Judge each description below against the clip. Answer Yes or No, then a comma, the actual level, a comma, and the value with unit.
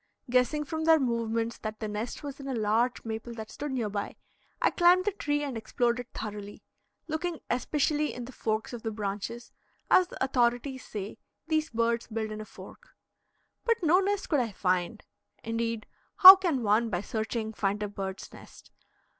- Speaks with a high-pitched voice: Yes, high, 235 Hz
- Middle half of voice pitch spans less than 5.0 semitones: No, average, 5.3 semitones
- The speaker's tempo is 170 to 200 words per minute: Yes, average, 180 wpm